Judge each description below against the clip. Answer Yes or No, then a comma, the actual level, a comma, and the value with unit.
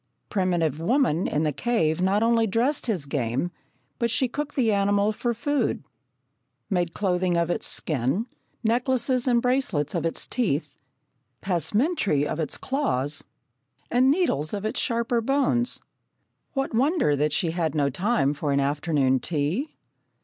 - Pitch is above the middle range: Yes, high, 195 Hz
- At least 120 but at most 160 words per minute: Yes, average, 145 wpm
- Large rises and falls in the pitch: Yes, wide, 8.0 semitones